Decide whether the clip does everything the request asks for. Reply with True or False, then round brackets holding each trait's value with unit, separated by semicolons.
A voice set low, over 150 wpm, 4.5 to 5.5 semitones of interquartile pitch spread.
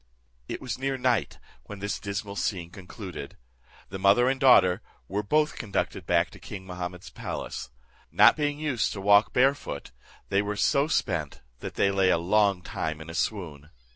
True (100 Hz; 175 wpm; 5.2 semitones)